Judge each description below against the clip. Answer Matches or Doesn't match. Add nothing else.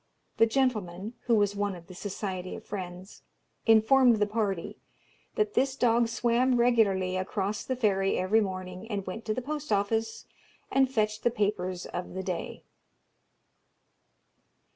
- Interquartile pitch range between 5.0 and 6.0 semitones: Doesn't match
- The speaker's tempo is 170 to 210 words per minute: Doesn't match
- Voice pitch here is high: Matches